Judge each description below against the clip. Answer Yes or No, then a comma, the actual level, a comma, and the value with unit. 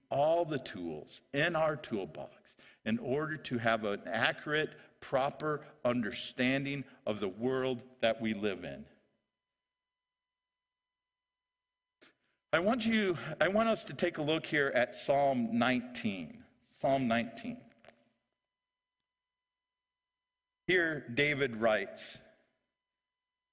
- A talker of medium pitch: Yes, medium, 160 Hz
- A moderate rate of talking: No, slow, 100 wpm